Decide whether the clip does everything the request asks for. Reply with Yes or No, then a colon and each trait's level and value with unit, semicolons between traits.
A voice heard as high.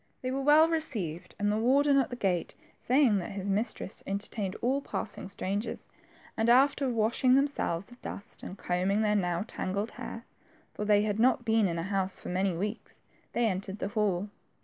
Yes: high, 210 Hz